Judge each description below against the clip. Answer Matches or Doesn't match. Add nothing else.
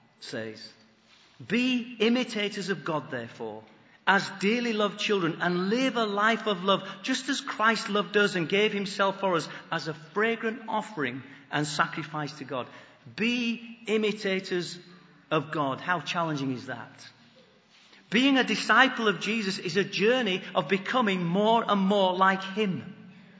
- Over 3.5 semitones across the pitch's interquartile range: Matches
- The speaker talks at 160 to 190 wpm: Doesn't match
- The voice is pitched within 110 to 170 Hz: Doesn't match